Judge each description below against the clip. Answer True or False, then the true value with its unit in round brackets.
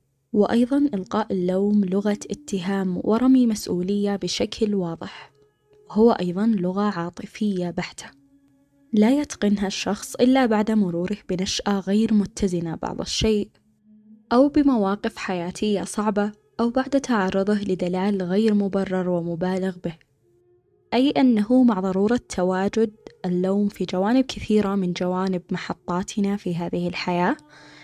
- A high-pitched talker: True (200 Hz)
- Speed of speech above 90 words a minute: True (110 wpm)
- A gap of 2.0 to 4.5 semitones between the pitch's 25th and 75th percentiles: True (3.0 semitones)